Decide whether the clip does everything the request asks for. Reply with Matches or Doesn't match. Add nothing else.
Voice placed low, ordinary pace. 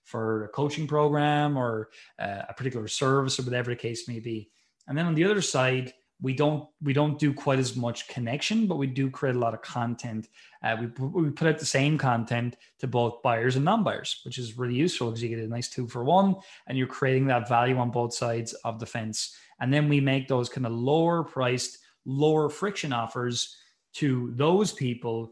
Doesn't match